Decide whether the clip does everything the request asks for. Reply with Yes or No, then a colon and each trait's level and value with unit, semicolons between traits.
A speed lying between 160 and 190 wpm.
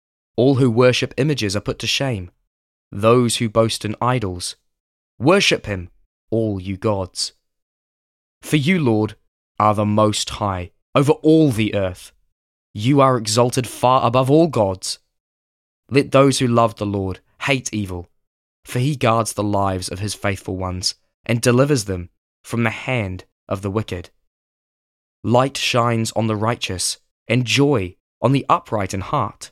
No: average, 150 wpm